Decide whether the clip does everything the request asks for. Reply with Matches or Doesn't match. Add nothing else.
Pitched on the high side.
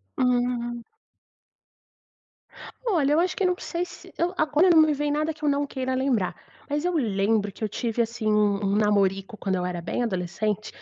Matches